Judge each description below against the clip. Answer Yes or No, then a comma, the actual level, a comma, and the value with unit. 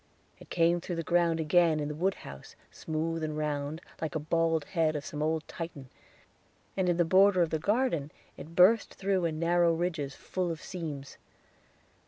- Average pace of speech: Yes, average, 180 wpm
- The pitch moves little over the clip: Yes, narrow, 2.2 semitones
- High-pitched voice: No, medium, 165 Hz